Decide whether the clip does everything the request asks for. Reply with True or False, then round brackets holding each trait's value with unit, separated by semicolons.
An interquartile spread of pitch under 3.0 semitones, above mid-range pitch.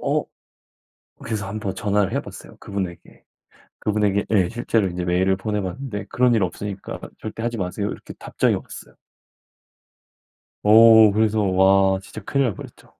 False (2.4 semitones; 105 Hz)